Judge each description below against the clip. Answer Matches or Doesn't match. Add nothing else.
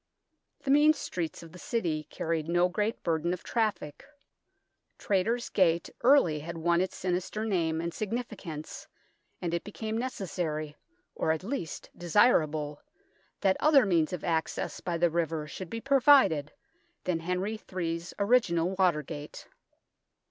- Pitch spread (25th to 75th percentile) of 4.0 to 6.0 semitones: Matches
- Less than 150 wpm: Matches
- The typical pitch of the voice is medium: Matches